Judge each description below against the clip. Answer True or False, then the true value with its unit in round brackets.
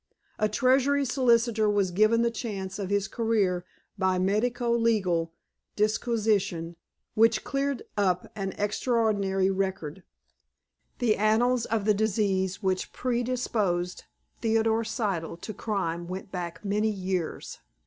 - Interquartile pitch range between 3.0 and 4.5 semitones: True (3.4 semitones)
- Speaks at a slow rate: True (120 wpm)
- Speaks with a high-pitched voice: True (210 Hz)